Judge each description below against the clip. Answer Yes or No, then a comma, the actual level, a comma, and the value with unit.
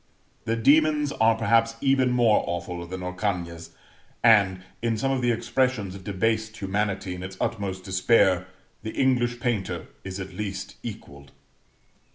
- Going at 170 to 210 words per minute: No, average, 145 wpm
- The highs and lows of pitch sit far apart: No, average, 4.1 semitones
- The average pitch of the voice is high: No, low, 105 Hz